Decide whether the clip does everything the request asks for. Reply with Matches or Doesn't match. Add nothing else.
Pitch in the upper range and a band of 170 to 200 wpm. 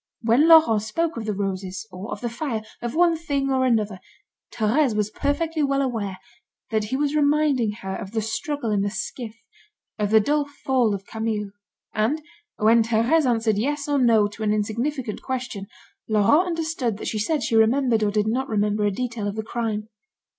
Matches